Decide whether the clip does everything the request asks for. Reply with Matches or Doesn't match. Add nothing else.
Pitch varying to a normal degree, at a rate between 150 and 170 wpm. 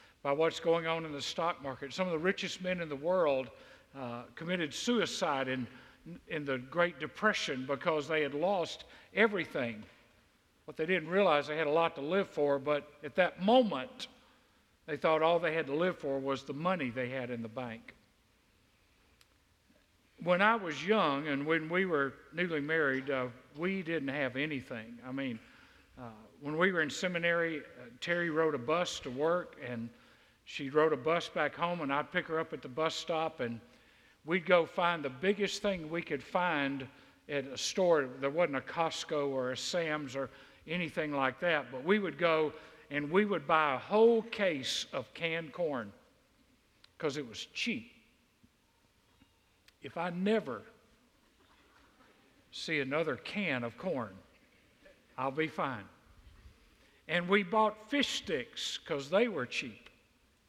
Matches